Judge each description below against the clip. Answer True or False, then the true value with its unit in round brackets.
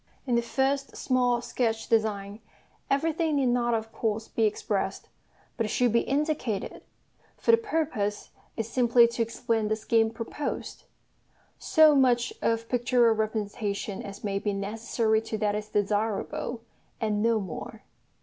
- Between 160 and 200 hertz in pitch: False (225 Hz)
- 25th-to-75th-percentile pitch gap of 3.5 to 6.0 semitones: False (2.6 semitones)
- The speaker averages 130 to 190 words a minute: True (145 wpm)